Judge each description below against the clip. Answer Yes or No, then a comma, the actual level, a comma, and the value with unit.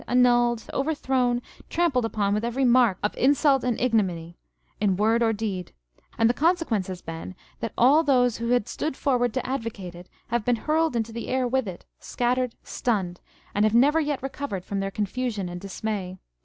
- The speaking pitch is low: No, high, 235 Hz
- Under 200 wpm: Yes, average, 175 wpm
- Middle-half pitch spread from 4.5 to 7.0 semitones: No, average, 4.1 semitones